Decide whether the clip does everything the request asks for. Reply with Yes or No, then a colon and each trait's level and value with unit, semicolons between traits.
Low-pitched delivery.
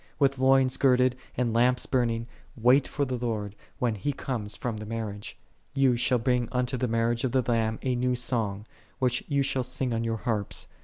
Yes: low, 125 Hz